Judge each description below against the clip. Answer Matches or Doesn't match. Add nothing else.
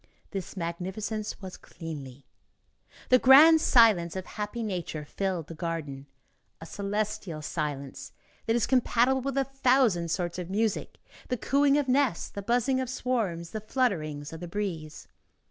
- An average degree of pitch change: Doesn't match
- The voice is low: Doesn't match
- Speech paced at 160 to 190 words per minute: Doesn't match